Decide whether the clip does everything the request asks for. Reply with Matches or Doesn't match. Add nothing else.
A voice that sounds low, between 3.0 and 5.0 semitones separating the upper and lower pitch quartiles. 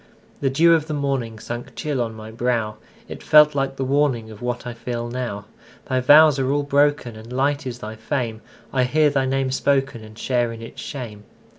Matches